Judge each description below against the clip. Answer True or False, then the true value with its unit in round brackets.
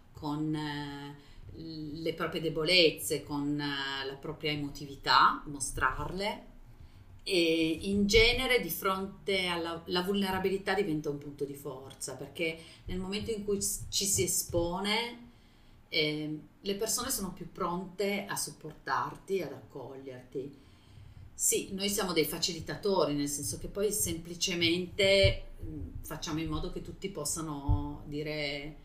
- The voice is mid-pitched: True (160 Hz)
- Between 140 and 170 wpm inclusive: False (120 wpm)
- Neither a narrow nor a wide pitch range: True (4.8 semitones)